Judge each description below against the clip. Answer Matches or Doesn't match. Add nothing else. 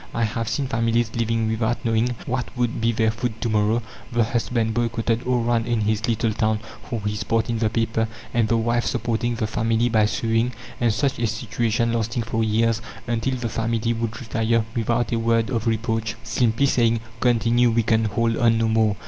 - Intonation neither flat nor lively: Doesn't match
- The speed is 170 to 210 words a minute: Matches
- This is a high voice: Doesn't match